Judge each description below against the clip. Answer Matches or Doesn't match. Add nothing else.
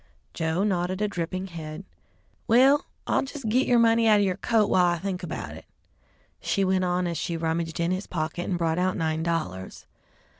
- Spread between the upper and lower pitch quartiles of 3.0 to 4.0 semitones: Matches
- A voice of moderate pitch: Matches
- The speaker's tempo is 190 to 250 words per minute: Matches